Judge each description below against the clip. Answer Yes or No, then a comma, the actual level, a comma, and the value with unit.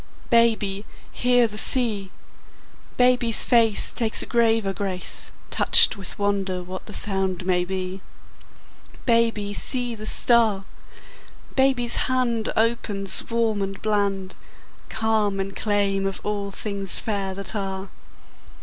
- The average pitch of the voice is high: Yes, high, 205 Hz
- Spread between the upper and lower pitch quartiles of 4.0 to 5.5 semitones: No, average, 2.9 semitones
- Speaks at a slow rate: Yes, slow, 120 wpm